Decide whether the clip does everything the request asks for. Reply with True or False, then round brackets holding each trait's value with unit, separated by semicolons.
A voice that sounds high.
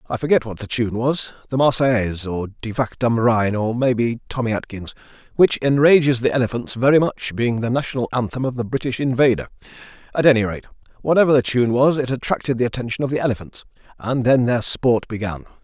False (120 Hz)